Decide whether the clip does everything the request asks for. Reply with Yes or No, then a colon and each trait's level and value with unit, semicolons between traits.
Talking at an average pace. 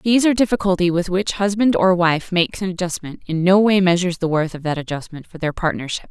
No: fast, 235 wpm